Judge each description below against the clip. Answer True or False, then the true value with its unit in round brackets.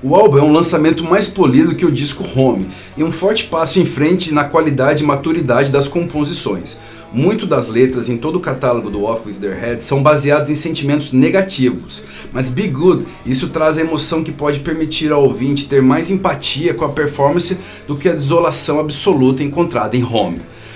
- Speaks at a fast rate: True (190 wpm)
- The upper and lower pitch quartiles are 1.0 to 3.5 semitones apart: False (4.0 semitones)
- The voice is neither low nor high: True (150 Hz)